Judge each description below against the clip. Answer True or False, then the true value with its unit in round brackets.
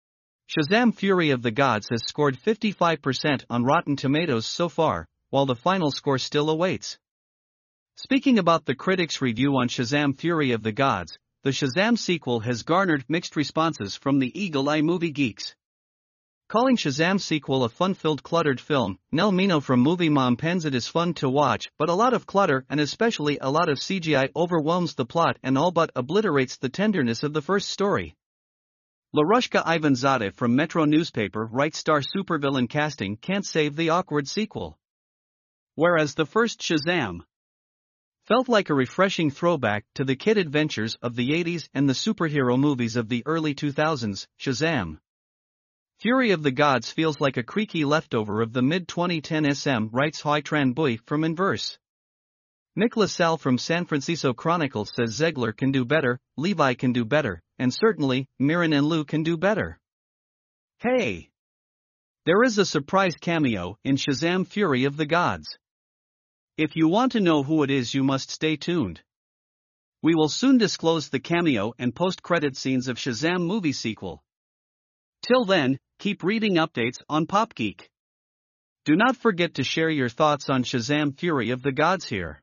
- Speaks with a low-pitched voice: False (150 Hz)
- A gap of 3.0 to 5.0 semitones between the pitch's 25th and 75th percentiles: True (4.7 semitones)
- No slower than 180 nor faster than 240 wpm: False (165 wpm)